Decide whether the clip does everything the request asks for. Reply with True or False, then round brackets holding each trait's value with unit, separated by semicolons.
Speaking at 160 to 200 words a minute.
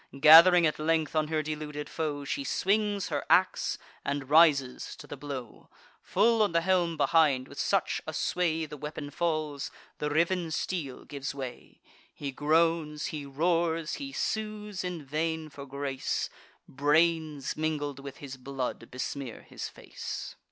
False (150 wpm)